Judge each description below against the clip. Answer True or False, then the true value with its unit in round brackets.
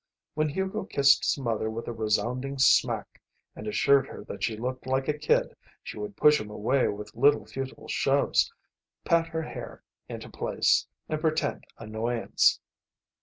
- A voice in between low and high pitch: False (130 Hz)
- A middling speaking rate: True (160 wpm)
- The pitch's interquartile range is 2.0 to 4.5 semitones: False (5.1 semitones)